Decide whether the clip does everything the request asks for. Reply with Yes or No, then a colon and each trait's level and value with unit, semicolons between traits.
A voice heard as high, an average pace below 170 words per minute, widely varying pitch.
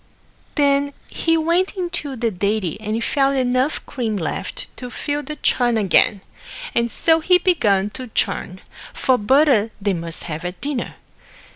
Yes: very high, 250 Hz; average, 150 wpm; wide, 6.1 semitones